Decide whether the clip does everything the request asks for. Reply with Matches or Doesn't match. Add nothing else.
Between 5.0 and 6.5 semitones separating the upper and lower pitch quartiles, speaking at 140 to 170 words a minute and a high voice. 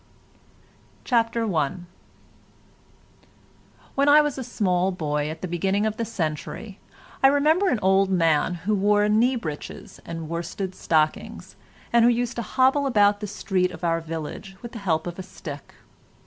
Matches